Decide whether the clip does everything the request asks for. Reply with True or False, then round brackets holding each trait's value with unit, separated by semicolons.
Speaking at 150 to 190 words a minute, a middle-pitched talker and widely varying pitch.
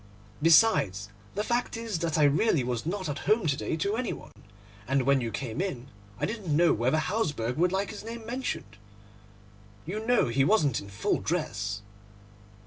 True (180 wpm; 160 Hz; 8.8 semitones)